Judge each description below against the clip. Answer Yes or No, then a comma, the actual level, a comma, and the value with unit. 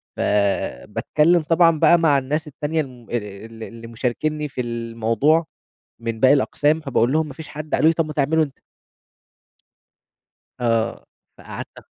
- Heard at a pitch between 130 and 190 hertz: Yes, medium, 140 Hz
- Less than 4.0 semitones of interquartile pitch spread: No, average, 5.0 semitones